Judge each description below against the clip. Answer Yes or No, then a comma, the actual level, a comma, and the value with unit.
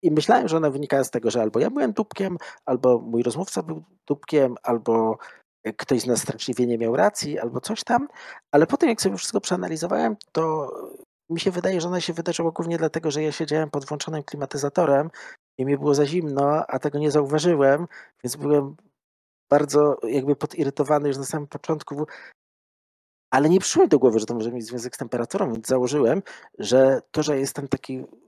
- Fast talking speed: Yes, fast, 185 wpm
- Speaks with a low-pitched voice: No, medium, 150 Hz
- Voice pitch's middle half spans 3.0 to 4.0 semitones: Yes, average, 3.6 semitones